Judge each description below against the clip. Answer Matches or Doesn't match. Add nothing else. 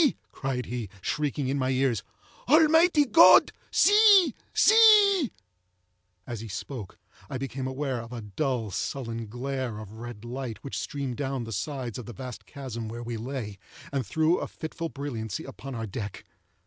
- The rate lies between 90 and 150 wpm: Doesn't match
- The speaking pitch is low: Matches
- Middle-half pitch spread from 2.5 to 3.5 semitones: Doesn't match